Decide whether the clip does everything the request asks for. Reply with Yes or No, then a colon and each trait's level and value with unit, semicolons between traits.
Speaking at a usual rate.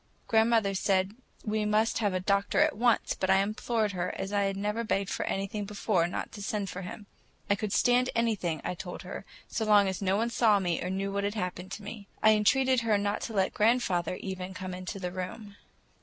No: fast, 215 wpm